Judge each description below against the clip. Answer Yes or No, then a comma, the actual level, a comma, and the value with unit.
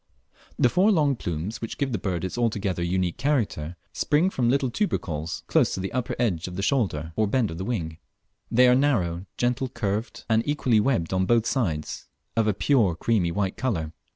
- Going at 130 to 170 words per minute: No, average, 200 wpm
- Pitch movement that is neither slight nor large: No, wide, 6.1 semitones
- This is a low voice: Yes, low, 110 Hz